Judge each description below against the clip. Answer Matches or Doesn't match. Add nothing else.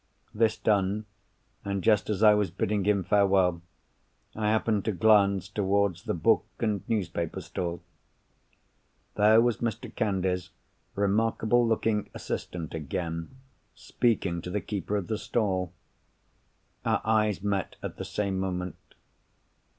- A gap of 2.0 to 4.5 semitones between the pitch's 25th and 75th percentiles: Matches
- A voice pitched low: Matches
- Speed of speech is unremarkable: Doesn't match